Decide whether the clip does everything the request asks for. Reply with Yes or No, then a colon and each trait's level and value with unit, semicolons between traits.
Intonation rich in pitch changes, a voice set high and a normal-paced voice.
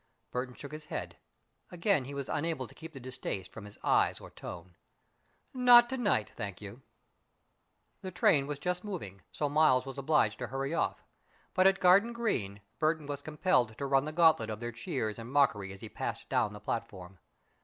No: wide, 6.9 semitones; medium, 140 Hz; average, 190 wpm